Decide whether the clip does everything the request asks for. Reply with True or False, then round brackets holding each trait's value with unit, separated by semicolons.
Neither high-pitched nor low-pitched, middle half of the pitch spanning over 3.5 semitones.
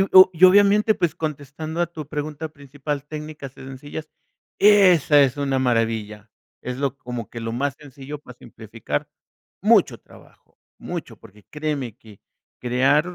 True (145 Hz; 3.9 semitones)